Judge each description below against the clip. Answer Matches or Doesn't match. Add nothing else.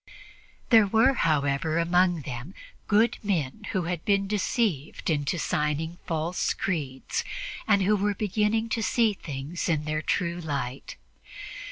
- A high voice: Doesn't match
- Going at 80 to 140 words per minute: Matches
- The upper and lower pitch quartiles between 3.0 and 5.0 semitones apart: Doesn't match